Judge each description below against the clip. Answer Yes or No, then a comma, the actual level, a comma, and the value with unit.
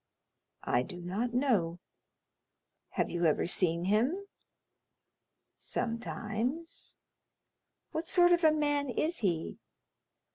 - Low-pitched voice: No, high, 235 Hz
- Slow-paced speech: Yes, slow, 100 wpm